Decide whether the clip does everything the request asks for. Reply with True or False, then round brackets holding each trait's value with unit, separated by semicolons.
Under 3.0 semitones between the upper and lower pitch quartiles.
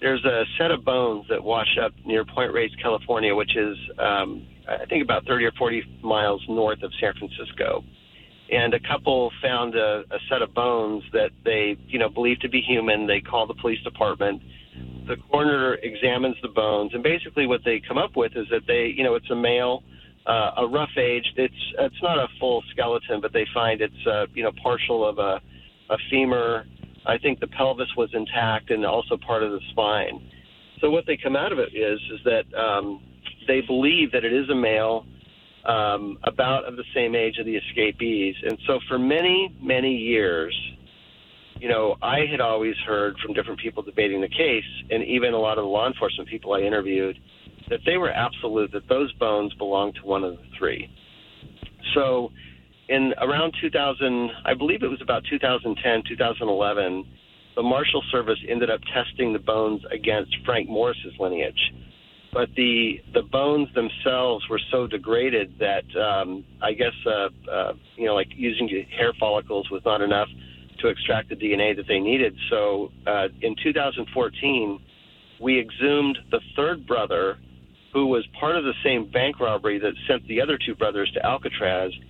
False (4.4 semitones)